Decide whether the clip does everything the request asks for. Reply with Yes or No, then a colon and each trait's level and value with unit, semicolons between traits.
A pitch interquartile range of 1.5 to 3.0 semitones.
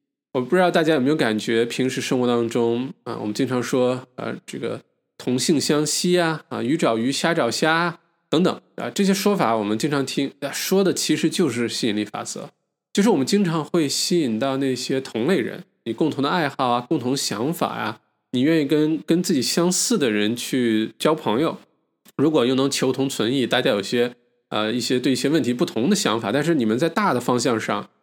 No: wide, 5.6 semitones